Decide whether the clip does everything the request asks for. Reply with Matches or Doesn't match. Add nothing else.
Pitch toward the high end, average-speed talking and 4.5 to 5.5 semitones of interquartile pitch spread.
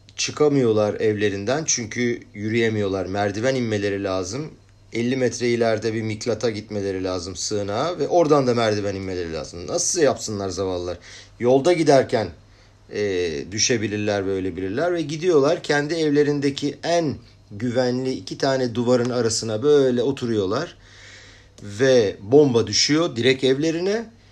Doesn't match